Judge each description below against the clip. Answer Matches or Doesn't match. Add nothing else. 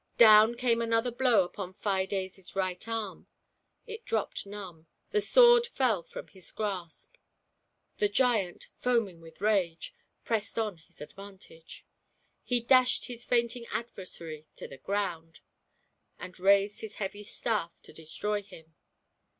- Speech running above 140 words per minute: Doesn't match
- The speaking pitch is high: Matches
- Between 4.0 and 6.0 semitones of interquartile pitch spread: Matches